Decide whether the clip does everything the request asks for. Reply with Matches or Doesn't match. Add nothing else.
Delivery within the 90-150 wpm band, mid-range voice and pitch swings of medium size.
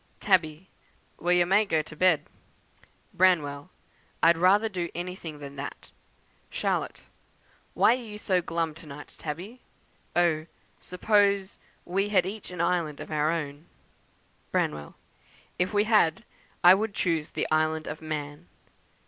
Matches